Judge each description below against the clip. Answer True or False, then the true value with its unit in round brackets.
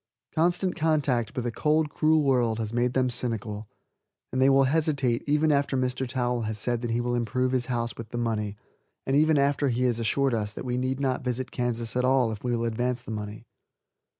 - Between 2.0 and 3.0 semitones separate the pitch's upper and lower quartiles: True (2.7 semitones)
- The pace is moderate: False (215 wpm)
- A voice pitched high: False (125 Hz)